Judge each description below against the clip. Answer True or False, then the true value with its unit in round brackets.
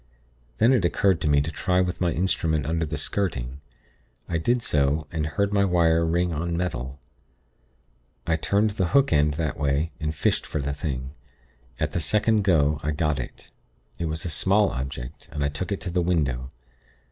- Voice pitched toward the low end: True (80 Hz)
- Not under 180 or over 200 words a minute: True (190 wpm)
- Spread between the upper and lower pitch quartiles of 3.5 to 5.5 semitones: True (3.8 semitones)